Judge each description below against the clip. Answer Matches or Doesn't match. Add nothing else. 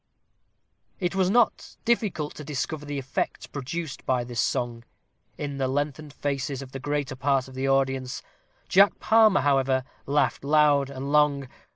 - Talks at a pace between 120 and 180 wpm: Matches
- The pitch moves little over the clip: Matches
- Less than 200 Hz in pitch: Matches